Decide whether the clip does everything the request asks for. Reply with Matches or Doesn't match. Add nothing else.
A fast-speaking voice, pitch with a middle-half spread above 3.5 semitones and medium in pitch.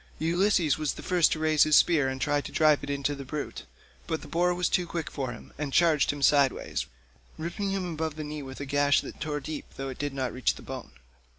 Doesn't match